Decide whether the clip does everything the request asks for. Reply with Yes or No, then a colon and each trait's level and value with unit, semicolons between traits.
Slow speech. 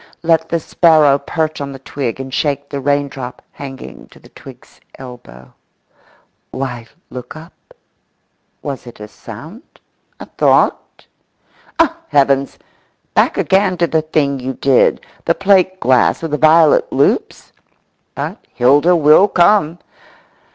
Yes: slow, 130 wpm